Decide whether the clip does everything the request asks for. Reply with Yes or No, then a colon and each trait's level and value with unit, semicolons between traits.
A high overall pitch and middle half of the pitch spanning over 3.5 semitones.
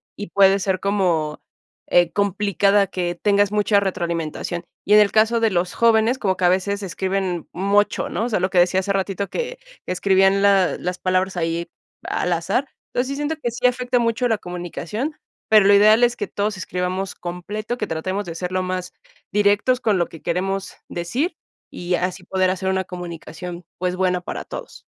No: high, 195 Hz; average, 2.7 semitones